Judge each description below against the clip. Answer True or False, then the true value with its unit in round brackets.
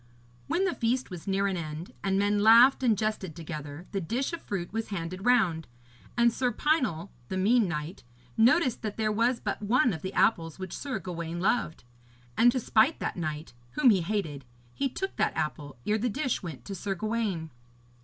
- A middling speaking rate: True (195 wpm)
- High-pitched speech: True (200 Hz)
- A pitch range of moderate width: False (5.9 semitones)